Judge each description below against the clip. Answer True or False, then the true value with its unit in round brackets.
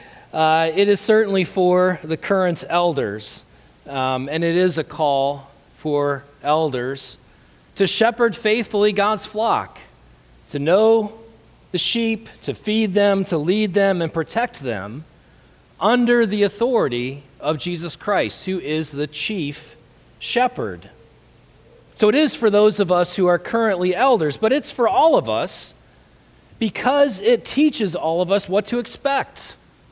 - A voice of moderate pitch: True (180 Hz)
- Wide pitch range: True (6.4 semitones)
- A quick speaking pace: False (140 wpm)